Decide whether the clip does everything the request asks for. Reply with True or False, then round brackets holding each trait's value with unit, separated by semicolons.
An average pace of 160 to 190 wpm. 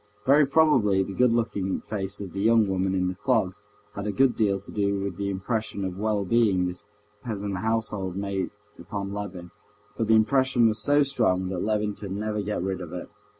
False (200 wpm)